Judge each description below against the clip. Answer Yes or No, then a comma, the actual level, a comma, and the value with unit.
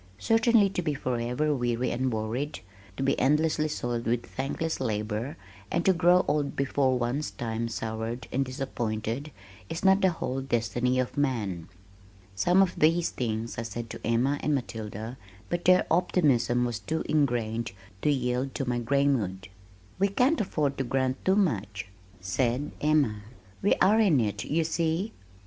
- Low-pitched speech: Yes, low, 130 Hz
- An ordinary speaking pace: Yes, average, 160 wpm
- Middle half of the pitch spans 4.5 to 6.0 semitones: Yes, average, 4.9 semitones